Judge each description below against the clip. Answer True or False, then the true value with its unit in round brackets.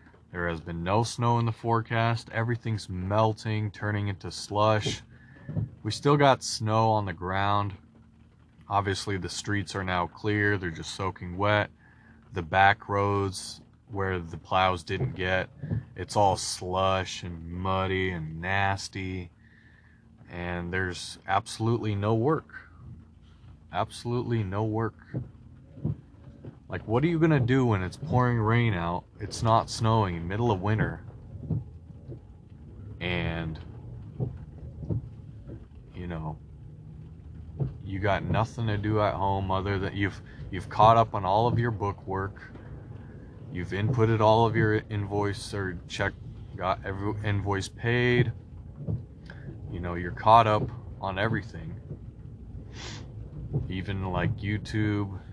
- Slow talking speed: True (125 wpm)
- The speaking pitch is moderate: False (105 Hz)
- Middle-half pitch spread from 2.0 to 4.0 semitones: True (3.5 semitones)